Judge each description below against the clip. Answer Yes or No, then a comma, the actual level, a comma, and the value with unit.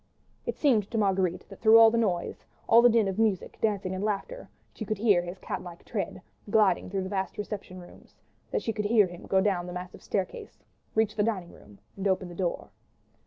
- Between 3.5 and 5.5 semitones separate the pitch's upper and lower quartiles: No, average, 2.9 semitones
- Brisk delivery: Yes, fast, 215 wpm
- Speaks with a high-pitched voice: Yes, high, 195 Hz